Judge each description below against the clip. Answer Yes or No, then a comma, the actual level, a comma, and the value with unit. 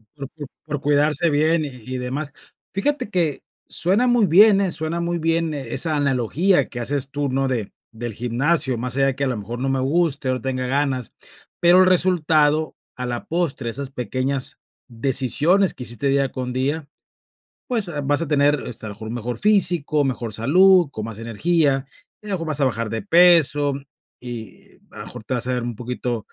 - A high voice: No, medium, 140 Hz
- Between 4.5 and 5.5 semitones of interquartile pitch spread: Yes, average, 4.8 semitones